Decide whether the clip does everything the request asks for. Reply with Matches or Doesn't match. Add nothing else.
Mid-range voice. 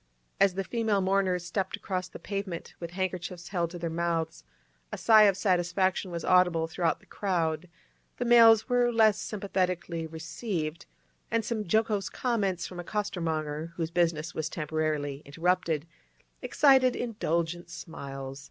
Matches